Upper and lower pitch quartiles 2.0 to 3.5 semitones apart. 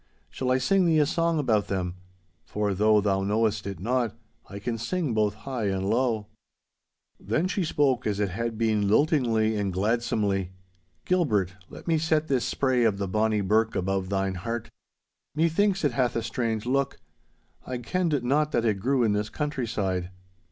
No: average, 5.1 semitones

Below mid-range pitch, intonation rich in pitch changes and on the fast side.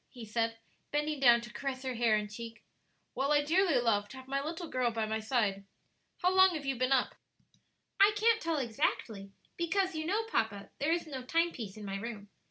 No: very high, 260 Hz; wide, 6.2 semitones; fast, 210 wpm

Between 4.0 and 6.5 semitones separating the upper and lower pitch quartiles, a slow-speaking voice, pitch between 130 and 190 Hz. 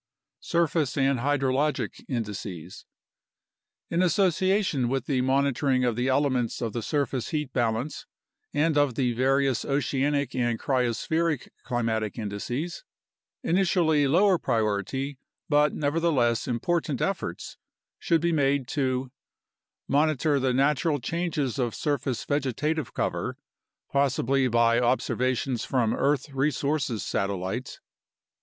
No: average, 3.6 semitones; slow, 110 wpm; low, 135 Hz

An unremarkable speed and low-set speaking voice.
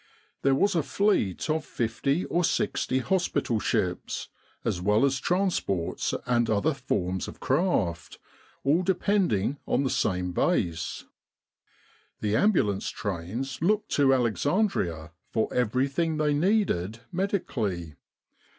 No: slow, 115 wpm; low, 130 Hz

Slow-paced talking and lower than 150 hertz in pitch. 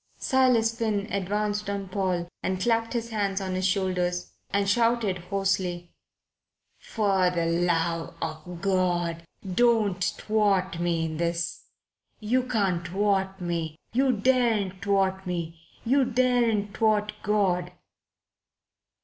No: slow, 115 wpm; high, 195 Hz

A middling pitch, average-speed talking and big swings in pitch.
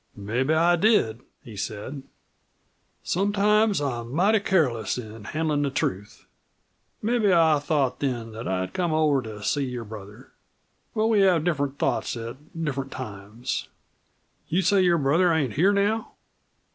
Yes: medium, 145 Hz; average, 145 wpm; wide, 7.3 semitones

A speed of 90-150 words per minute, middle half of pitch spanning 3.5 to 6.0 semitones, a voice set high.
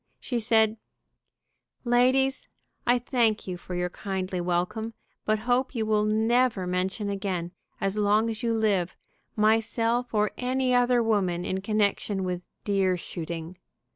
Yes: average, 140 wpm; average, 4.0 semitones; high, 215 Hz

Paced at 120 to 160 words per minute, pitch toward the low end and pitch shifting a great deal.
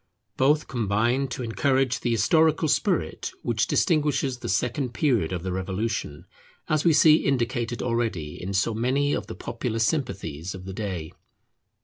Yes: average, 150 wpm; low, 120 Hz; wide, 5.9 semitones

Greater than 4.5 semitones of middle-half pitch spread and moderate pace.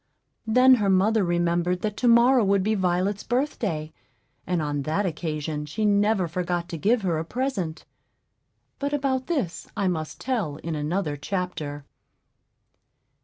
Yes: wide, 5.4 semitones; average, 145 wpm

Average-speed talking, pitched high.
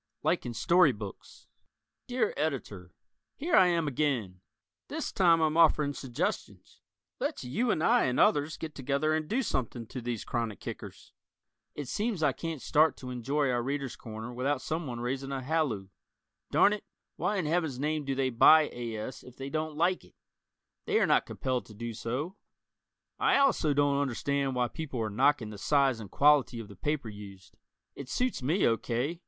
No: average, 180 wpm; medium, 140 Hz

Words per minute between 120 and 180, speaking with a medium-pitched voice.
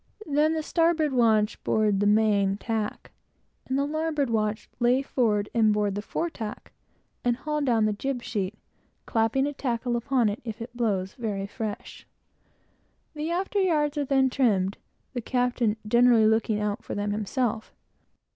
No: average, 160 wpm; high, 235 Hz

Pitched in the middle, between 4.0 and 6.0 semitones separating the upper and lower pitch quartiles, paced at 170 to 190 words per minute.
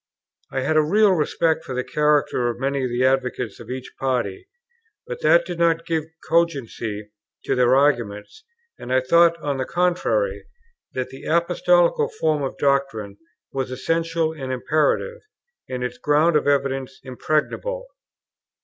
No: medium, 145 Hz; average, 4.6 semitones; average, 150 wpm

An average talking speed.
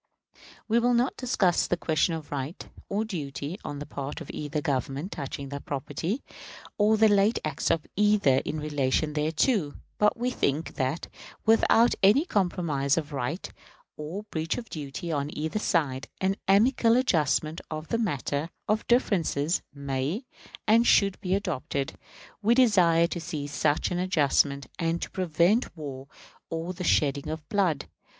Yes: average, 155 wpm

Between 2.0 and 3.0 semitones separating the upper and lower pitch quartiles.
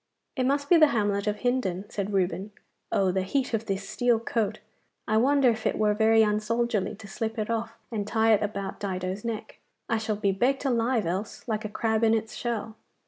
Yes: narrow, 2.4 semitones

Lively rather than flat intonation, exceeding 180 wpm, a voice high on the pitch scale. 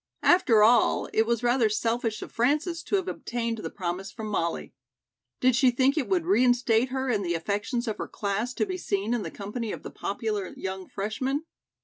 No: average, 3.7 semitones; average, 200 wpm; high, 230 Hz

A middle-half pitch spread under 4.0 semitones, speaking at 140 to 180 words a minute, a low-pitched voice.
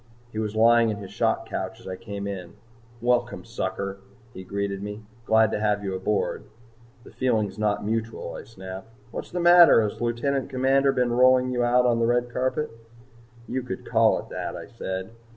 No: average, 3.6 semitones; average, 190 wpm; low, 115 Hz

